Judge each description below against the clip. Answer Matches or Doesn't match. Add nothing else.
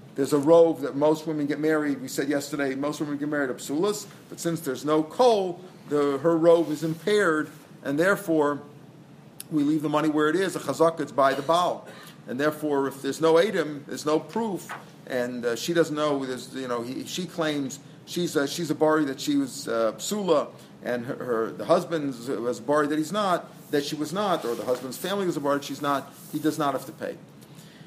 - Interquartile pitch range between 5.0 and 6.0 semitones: Doesn't match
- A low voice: Doesn't match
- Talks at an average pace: Doesn't match